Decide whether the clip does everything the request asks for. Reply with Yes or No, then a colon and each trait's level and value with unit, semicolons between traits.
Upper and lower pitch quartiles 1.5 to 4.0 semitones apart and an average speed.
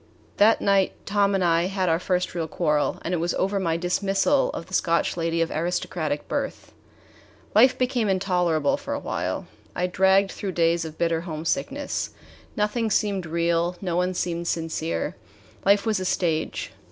Yes: average, 3.0 semitones; average, 165 wpm